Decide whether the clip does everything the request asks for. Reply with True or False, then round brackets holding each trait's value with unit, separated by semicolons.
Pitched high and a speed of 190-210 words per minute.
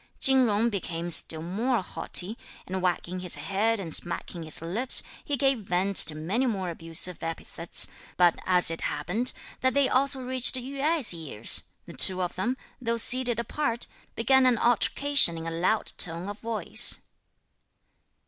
False (205 Hz; 160 wpm)